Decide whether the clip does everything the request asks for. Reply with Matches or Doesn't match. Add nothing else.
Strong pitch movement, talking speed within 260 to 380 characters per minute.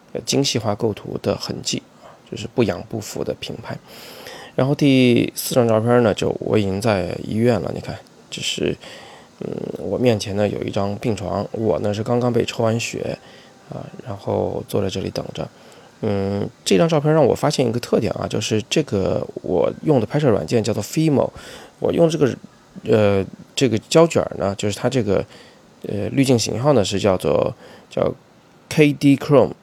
Doesn't match